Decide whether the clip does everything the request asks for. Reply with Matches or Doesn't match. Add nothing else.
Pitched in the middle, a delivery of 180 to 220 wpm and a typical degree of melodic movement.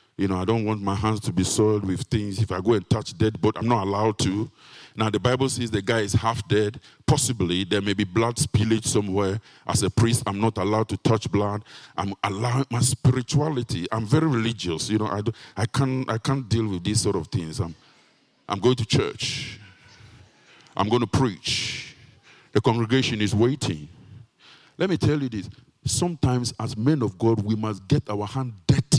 Doesn't match